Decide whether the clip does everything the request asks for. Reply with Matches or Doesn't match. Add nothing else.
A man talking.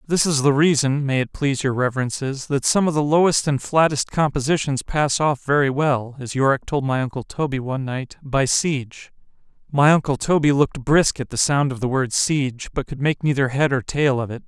Matches